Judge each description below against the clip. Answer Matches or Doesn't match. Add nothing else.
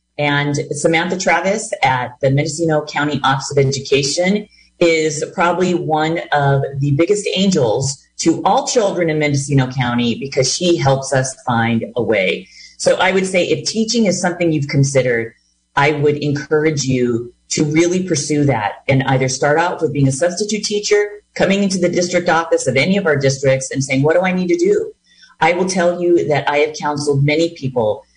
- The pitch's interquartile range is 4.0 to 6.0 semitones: Matches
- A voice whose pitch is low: Doesn't match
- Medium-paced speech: Matches